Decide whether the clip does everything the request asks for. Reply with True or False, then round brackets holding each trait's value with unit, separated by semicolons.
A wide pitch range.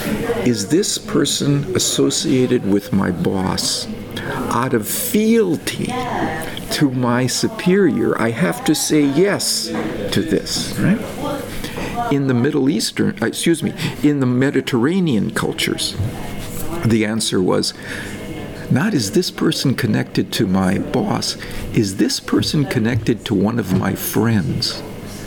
True (5.7 semitones)